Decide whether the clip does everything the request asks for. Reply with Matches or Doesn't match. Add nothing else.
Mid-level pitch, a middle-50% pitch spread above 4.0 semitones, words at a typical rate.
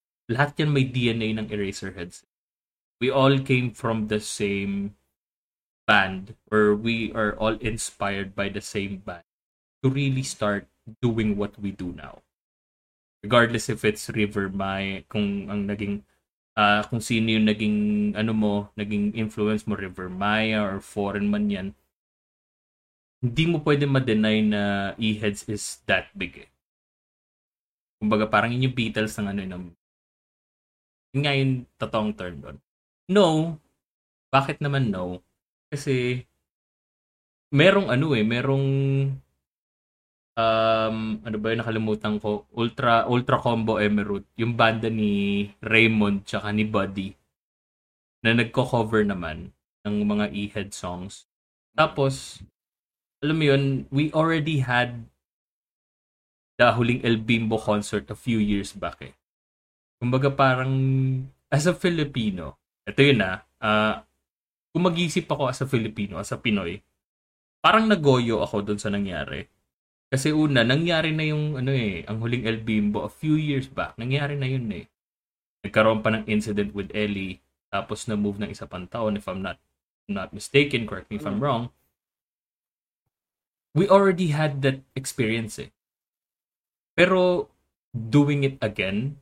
Doesn't match